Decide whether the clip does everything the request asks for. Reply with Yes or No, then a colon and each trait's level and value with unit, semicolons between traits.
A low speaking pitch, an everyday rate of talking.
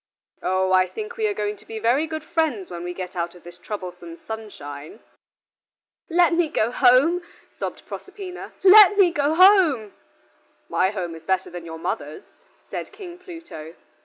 No: high, 225 Hz; average, 165 wpm